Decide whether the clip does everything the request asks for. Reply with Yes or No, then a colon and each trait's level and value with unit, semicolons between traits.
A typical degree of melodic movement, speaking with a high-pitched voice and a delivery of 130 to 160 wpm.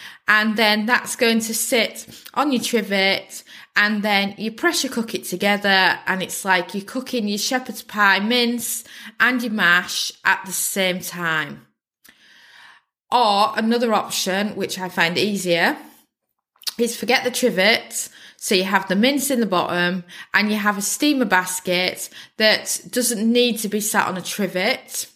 Yes: average, 4.0 semitones; high, 210 Hz; average, 155 wpm